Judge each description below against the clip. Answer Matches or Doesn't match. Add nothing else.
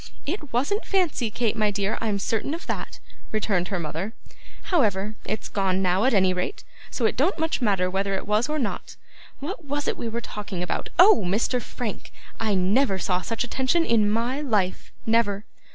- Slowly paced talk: Doesn't match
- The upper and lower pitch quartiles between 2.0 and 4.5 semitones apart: Doesn't match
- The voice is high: Matches